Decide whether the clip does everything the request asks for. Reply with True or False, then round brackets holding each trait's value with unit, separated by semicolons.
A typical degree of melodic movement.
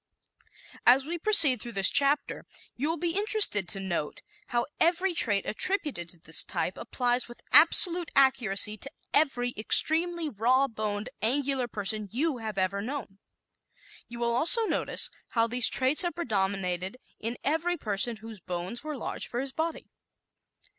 False (6.6 semitones)